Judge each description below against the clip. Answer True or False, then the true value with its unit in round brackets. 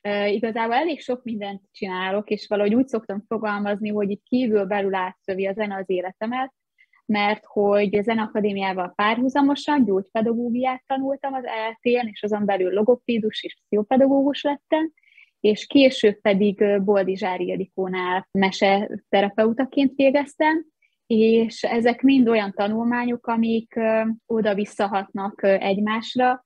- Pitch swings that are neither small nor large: True (3.7 semitones)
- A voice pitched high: True (220 Hz)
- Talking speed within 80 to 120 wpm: True (115 wpm)